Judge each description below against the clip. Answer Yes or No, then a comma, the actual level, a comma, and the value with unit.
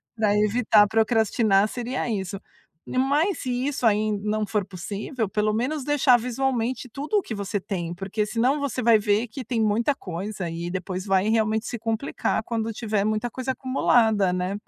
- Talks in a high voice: Yes, high, 220 Hz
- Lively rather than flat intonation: No, average, 3.5 semitones